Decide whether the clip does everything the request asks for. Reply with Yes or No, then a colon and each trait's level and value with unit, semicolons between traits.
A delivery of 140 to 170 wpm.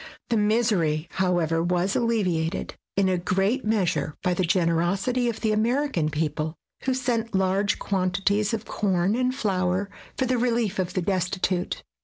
Yes: average, 150 wpm